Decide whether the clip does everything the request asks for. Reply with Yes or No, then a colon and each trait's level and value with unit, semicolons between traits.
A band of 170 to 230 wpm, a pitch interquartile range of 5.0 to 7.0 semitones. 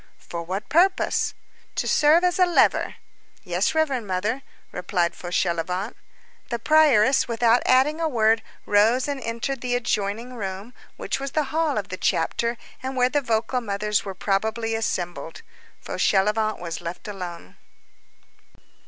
No: average, 140 wpm; average, 5.3 semitones